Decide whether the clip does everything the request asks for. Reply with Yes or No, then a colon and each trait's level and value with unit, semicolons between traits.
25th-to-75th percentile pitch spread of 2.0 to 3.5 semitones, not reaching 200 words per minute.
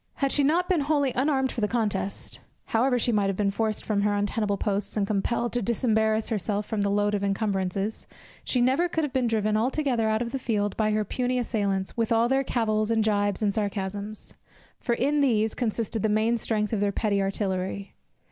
No: average, 2.9 semitones; fast, 205 wpm